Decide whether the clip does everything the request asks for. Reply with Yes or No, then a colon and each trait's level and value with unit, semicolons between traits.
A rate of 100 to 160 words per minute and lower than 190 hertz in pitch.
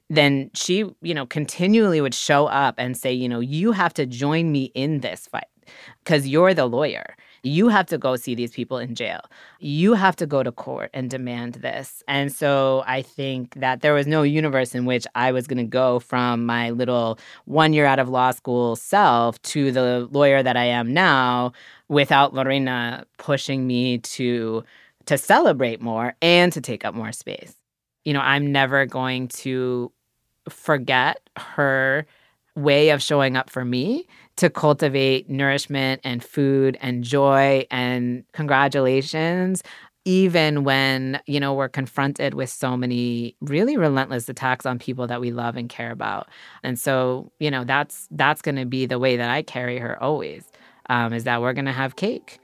No: average, 175 wpm; low, 135 Hz